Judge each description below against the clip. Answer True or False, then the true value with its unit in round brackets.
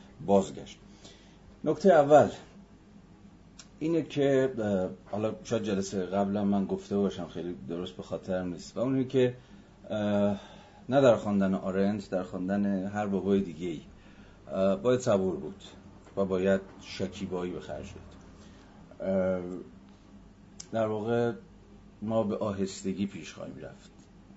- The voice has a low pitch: True (100 Hz)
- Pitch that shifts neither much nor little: False (2.0 semitones)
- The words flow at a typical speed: True (115 wpm)